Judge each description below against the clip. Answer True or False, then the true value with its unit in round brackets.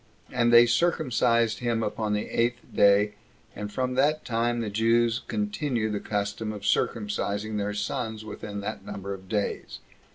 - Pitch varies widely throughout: False (2.4 semitones)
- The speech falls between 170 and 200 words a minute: False (155 wpm)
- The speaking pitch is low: True (110 Hz)